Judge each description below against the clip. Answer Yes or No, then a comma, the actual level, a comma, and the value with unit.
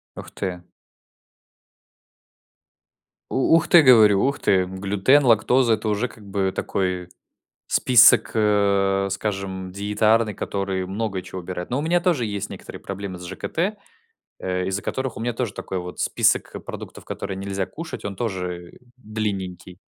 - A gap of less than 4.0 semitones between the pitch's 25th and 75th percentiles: Yes, average, 3.5 semitones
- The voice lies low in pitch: Yes, low, 100 Hz